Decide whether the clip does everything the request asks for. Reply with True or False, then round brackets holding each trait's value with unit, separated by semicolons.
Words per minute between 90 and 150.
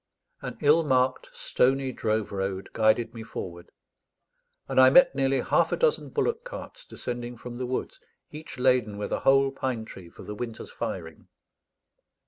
False (160 wpm)